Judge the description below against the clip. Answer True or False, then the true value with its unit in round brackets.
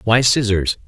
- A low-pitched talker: True (110 Hz)